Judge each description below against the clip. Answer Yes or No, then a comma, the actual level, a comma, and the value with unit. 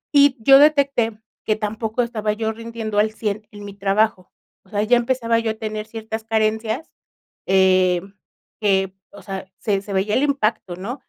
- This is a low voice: No, high, 215 Hz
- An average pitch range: No, narrow, 2.2 semitones